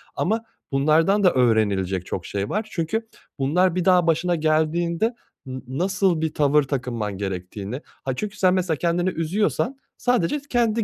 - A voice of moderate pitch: Yes, medium, 165 Hz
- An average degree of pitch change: No, wide, 6.3 semitones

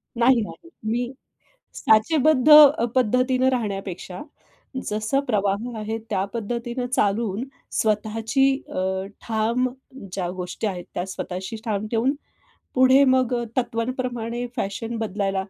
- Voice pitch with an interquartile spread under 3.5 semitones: No, average, 3.8 semitones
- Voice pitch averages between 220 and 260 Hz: Yes, high, 225 Hz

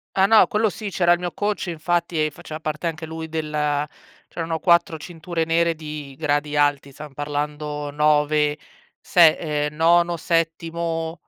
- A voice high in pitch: No, medium, 160 Hz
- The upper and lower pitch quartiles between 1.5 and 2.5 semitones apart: Yes, narrow, 2.2 semitones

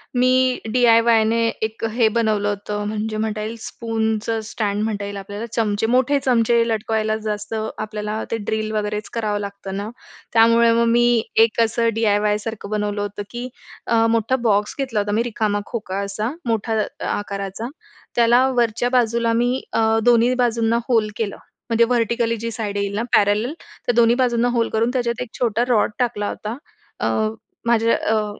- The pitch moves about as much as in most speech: No, narrow, 1.9 semitones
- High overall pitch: Yes, high, 225 Hz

